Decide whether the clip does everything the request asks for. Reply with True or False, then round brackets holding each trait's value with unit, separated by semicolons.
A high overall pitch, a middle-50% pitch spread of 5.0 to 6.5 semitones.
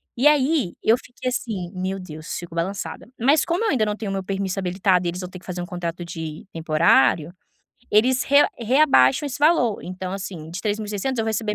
True (195 Hz; 5.6 semitones)